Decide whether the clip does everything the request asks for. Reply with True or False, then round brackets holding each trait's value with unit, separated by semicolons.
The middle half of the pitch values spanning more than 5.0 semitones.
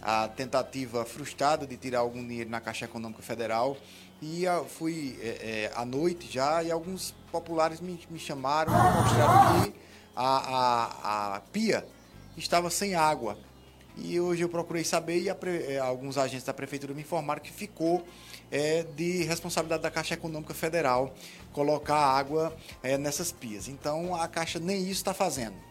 True (5.6 semitones)